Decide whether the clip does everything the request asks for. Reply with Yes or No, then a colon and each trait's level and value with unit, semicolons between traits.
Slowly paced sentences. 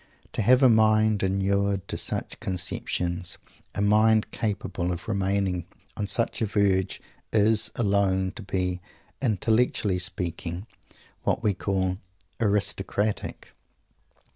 Yes: slow, 115 wpm